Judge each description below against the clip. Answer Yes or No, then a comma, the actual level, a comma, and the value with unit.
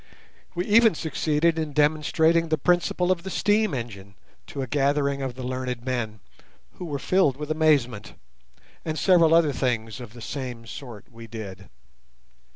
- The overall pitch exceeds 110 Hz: Yes, medium, 140 Hz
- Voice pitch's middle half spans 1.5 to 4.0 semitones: No, average, 5.2 semitones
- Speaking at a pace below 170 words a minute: Yes, average, 160 wpm